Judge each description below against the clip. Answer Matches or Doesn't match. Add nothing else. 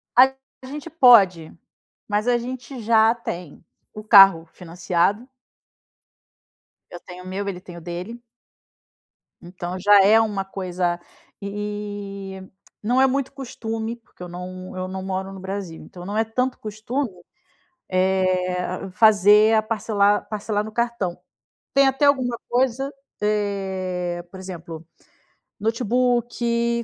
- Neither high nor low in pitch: Doesn't match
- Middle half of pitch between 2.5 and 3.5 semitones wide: Doesn't match